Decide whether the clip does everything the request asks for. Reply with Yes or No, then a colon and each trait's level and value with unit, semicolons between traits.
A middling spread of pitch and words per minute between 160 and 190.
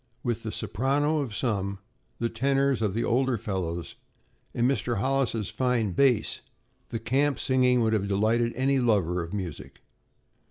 No: average, 4.5 semitones; average, 150 wpm